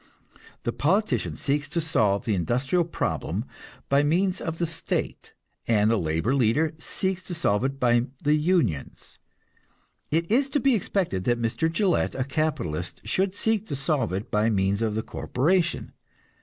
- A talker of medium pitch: Yes, medium, 145 Hz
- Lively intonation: Yes, wide, 7.5 semitones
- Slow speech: No, average, 160 wpm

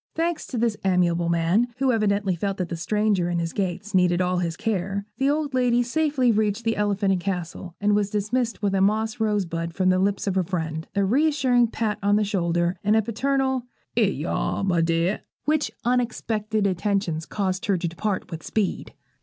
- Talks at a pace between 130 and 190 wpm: No, average, 200 wpm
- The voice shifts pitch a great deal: No, average, 4.0 semitones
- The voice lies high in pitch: Yes, high, 200 Hz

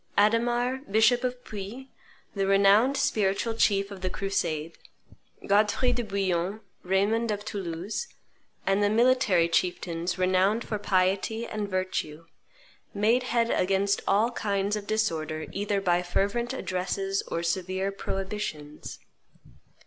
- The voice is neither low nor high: No, high, 200 Hz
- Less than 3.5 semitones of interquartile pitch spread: Yes, average, 3.0 semitones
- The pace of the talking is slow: Yes, slow, 120 wpm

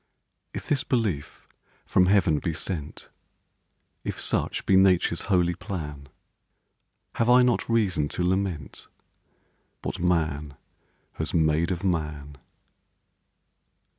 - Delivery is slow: Yes, slow, 105 wpm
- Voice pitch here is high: No, very low, 85 Hz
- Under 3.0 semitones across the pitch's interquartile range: No, average, 4.1 semitones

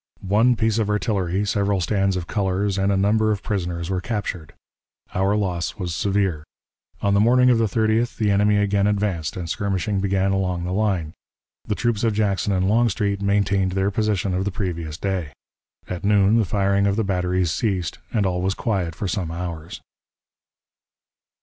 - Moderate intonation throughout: No, narrow, 2.3 semitones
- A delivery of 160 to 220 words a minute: Yes, average, 175 wpm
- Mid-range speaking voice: No, low, 100 Hz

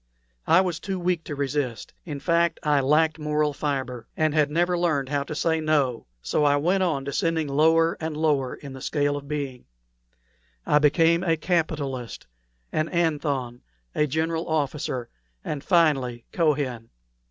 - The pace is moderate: Yes, average, 155 wpm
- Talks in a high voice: No, medium, 150 Hz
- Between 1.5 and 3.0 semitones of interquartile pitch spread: Yes, average, 2.7 semitones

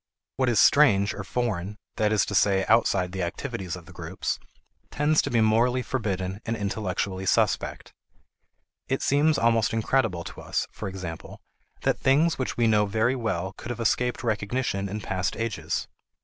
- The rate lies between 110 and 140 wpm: No, average, 165 wpm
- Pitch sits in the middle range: No, low, 110 Hz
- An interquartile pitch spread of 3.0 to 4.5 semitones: Yes, average, 4.1 semitones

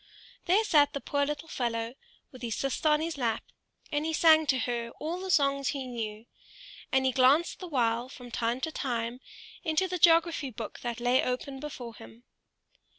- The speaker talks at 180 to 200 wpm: Yes, average, 185 wpm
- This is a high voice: Yes, very high, 265 Hz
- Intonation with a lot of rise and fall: No, average, 4.6 semitones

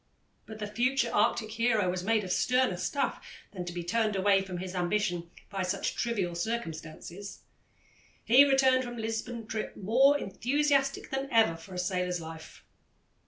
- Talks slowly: No, average, 165 wpm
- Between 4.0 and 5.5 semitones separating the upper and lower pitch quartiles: Yes, average, 5.1 semitones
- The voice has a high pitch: Yes, high, 210 Hz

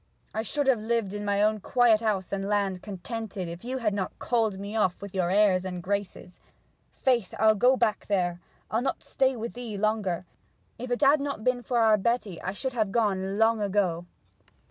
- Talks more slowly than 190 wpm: No, average, 200 wpm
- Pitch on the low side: No, high, 210 Hz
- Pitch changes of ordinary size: Yes, average, 3.4 semitones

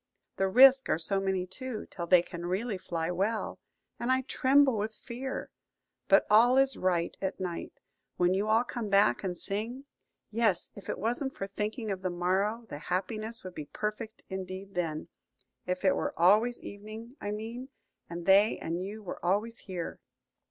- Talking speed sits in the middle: Yes, average, 175 wpm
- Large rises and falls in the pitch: No, average, 3.9 semitones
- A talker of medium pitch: No, high, 200 Hz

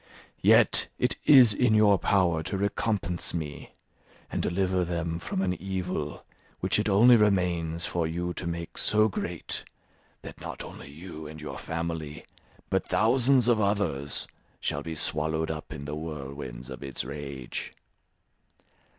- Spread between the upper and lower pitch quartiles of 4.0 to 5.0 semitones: Yes, average, 4.4 semitones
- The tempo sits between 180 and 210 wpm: No, average, 145 wpm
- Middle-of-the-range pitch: No, very low, 85 Hz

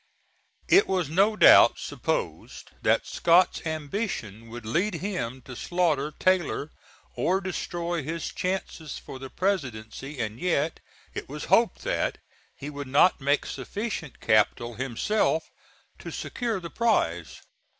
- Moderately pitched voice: Yes, medium, 160 Hz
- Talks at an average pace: No, slow, 130 wpm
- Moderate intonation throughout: No, wide, 6.1 semitones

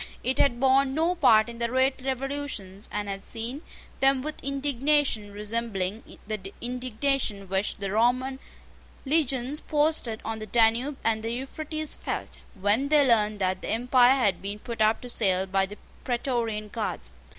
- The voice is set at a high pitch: Yes, high, 235 Hz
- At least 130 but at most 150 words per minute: No, average, 160 wpm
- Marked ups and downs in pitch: No, average, 4.3 semitones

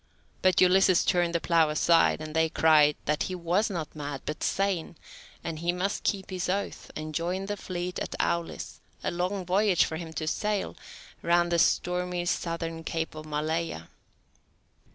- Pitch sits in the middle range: Yes, medium, 170 Hz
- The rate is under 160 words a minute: No, average, 170 wpm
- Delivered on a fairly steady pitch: Yes, narrow, 2.3 semitones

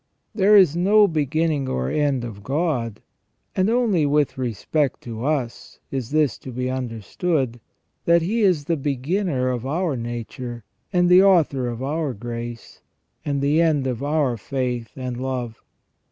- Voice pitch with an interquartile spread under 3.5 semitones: No, average, 5.2 semitones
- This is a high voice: No, medium, 140 Hz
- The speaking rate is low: No, average, 155 wpm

